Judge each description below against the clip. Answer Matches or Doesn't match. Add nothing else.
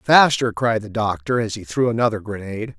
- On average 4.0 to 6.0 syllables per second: Matches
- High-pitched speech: Doesn't match